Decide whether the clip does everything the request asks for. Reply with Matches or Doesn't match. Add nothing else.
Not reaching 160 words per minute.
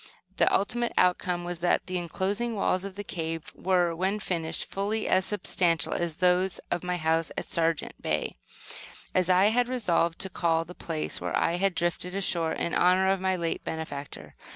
Doesn't match